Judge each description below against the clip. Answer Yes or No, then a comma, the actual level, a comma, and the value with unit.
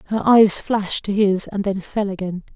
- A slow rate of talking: No, fast, 210 wpm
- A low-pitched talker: No, high, 200 Hz